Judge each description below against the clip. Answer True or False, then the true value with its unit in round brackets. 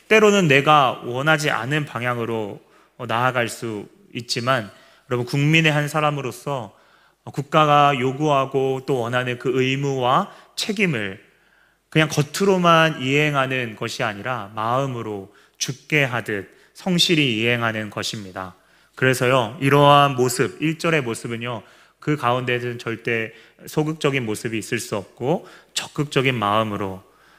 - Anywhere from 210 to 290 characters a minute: True (280 characters per minute)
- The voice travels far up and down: False (4.2 semitones)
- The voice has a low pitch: True (130 Hz)